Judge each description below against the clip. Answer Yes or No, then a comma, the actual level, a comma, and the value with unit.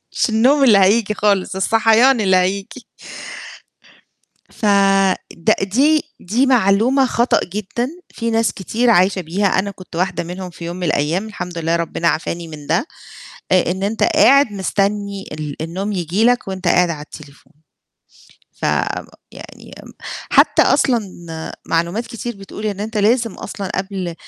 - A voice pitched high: Yes, high, 195 Hz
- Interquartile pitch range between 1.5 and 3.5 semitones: No, average, 4.1 semitones